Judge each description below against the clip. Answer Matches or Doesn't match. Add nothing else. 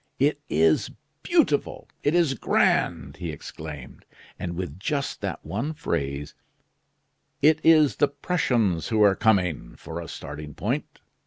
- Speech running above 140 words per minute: Doesn't match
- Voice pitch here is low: Matches